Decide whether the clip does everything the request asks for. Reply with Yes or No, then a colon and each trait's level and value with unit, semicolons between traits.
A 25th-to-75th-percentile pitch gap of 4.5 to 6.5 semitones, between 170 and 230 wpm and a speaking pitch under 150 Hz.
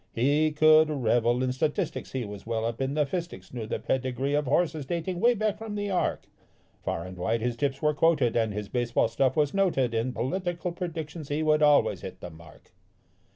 Yes: average, 5.3 semitones; fast, 205 wpm; medium, 140 Hz